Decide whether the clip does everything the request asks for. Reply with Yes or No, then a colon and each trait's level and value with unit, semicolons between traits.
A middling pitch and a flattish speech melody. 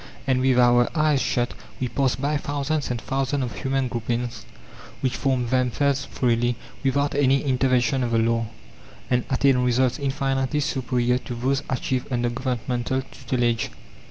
No: low, 130 Hz; narrow, 2.0 semitones